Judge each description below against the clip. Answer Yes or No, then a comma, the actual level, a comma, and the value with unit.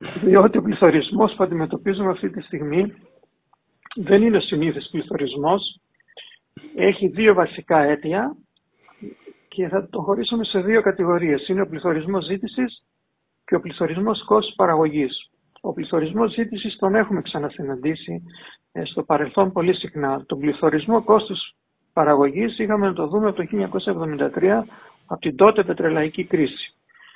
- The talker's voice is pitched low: No, high, 190 Hz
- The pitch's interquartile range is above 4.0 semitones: Yes, average, 5.1 semitones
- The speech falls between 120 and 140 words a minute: Yes, average, 125 wpm